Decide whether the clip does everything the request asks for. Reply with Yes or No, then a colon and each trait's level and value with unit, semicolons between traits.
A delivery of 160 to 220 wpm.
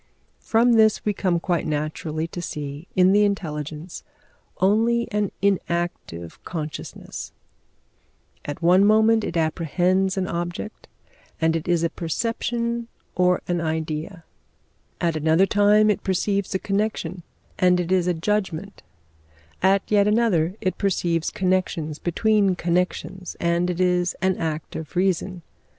No: slow, 135 wpm